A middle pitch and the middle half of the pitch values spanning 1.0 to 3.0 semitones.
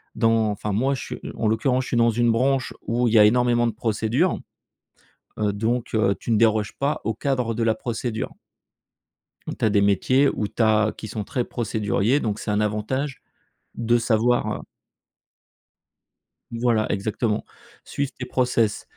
No: low, 115 Hz; narrow, 2.4 semitones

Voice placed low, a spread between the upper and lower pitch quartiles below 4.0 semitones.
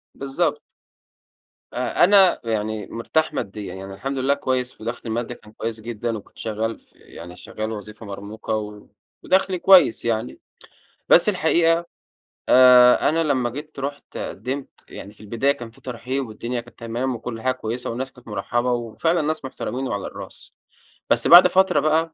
No: low, 125 Hz; average, 4.3 semitones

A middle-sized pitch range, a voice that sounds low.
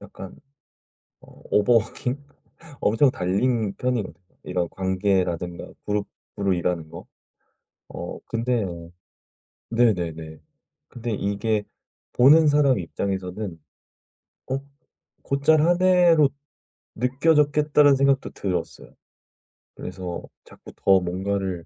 No: wide, 6.7 semitones; low, 105 Hz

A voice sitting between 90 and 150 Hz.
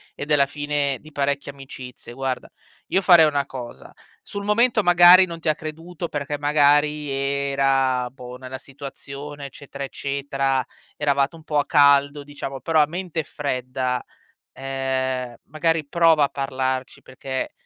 Yes: medium, 140 Hz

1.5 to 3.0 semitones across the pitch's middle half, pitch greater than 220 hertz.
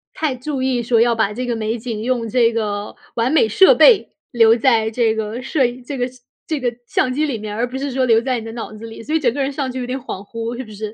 Yes: narrow, 2.6 semitones; high, 240 Hz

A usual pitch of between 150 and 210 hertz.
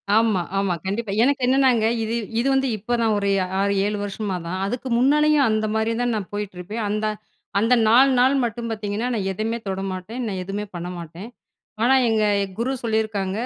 No: high, 220 Hz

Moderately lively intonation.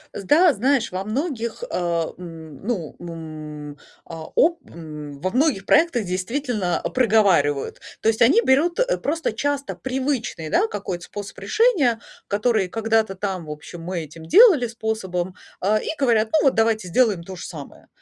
No: wide, 6.9 semitones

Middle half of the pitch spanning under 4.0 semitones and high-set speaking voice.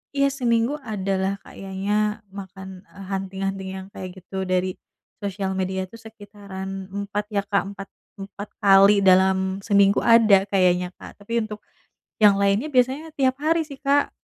Yes: narrow, 2.4 semitones; high, 200 Hz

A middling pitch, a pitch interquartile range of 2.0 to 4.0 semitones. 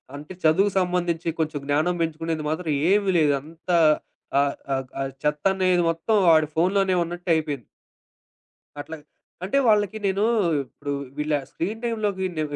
Yes: medium, 165 Hz; average, 3.7 semitones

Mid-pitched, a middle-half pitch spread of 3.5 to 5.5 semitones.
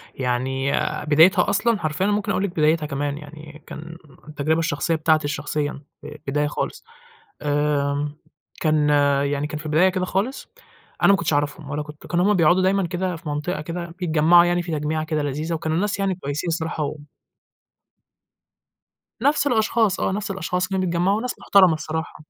Yes: medium, 160 Hz; average, 3.8 semitones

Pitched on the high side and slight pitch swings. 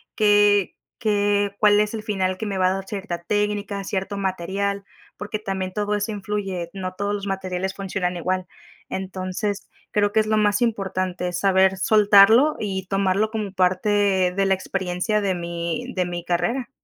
Yes: high, 195 Hz; narrow, 1.8 semitones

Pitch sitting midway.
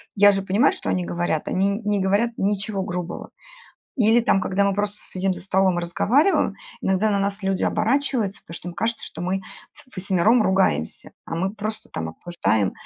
No: high, 195 Hz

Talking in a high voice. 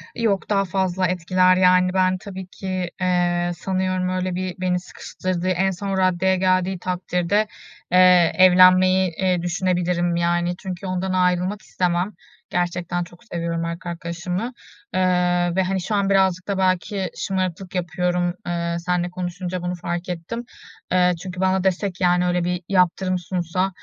No: medium, 180 Hz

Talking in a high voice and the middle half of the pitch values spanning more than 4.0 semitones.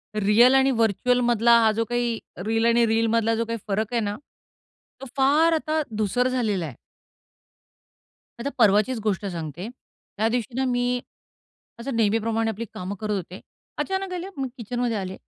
No: high, 230 Hz; average, 2.8 semitones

